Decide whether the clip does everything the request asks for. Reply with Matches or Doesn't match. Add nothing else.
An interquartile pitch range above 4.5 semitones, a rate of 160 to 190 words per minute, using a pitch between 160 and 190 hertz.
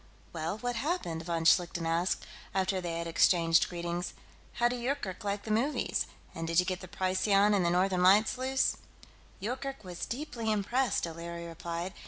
Matches